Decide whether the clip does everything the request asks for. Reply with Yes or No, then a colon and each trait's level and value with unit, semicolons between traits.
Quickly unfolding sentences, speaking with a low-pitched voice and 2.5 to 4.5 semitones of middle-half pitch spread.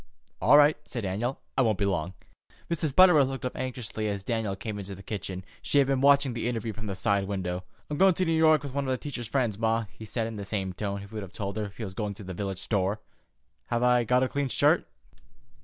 No: fast, 245 wpm; low, 110 Hz; average, 4.9 semitones